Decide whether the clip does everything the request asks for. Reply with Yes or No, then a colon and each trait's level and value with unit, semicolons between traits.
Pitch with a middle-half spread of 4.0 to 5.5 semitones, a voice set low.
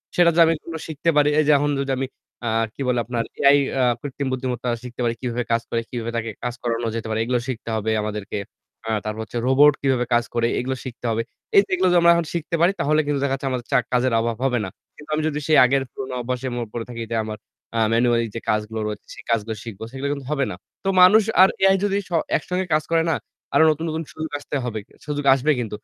Yes: average, 4.3 semitones; low, 130 Hz